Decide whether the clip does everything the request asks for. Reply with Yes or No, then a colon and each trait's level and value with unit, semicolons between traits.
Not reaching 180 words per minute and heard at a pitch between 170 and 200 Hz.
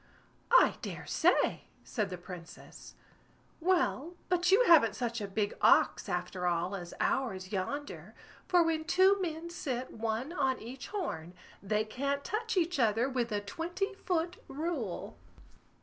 No: average, 145 wpm; very high, 265 Hz